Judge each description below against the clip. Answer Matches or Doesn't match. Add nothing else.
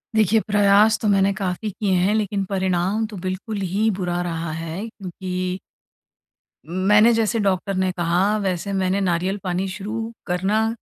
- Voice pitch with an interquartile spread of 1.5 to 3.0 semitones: Matches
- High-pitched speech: Matches